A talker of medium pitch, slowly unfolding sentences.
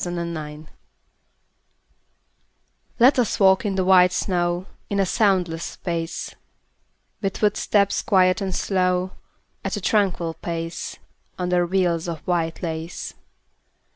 Yes: medium, 180 Hz; slow, 115 wpm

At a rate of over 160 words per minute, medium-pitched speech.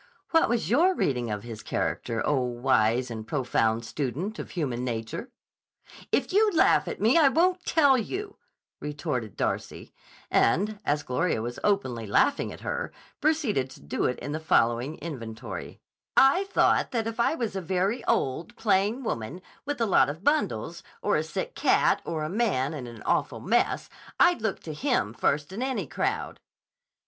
Yes: average, 170 wpm; medium, 165 Hz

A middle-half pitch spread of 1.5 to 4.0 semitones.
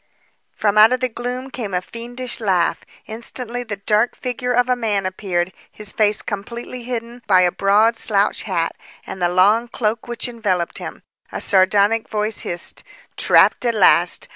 Yes: average, 3.5 semitones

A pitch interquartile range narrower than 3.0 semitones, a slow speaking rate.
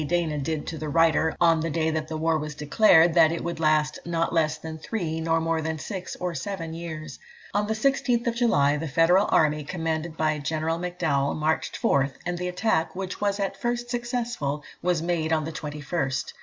No: narrow, 2.5 semitones; average, 195 wpm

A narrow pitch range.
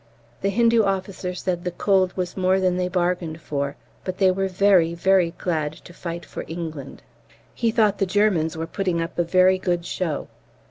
Yes: narrow, 2.3 semitones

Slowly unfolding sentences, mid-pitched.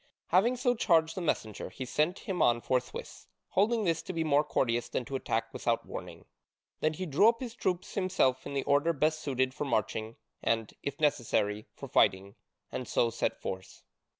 No: average, 185 wpm; medium, 145 Hz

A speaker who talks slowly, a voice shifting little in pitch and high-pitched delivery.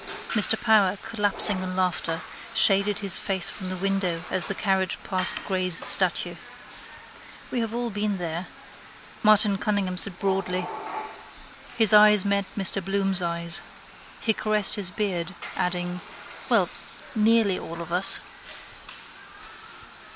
Yes: slow, 125 wpm; narrow, 2.2 semitones; high, 195 Hz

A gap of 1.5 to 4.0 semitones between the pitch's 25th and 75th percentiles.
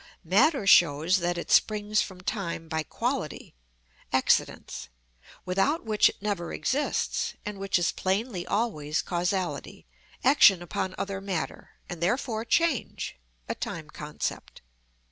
Yes: average, 3.7 semitones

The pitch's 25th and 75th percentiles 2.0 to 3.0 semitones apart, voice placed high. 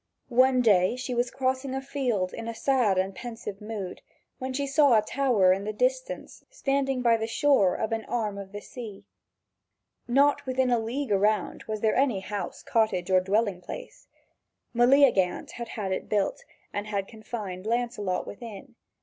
No: average, 4.3 semitones; high, 225 Hz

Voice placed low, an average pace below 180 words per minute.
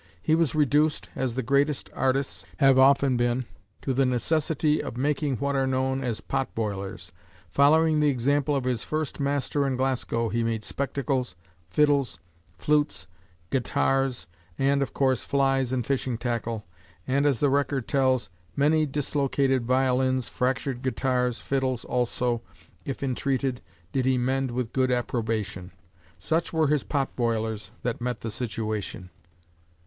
Yes: low, 130 Hz; average, 145 wpm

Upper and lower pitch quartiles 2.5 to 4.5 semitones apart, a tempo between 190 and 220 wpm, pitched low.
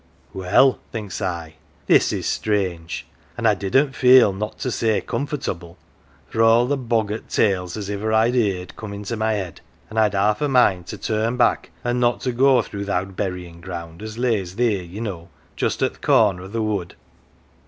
Yes: average, 3.8 semitones; average, 200 wpm; low, 105 Hz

